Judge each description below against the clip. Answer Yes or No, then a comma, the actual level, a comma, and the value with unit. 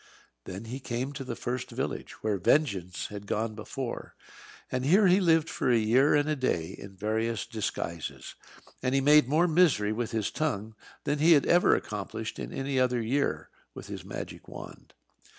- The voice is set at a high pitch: No, low, 125 Hz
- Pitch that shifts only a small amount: No, average, 5.2 semitones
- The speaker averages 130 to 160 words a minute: No, average, 180 wpm